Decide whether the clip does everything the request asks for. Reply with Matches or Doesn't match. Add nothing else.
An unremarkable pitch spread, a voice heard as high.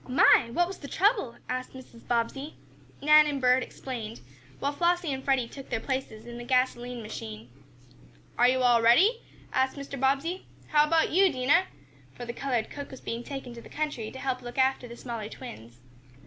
Matches